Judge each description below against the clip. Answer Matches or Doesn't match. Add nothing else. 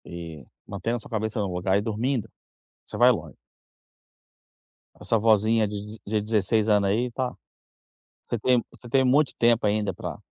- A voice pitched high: Doesn't match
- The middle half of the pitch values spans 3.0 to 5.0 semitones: Doesn't match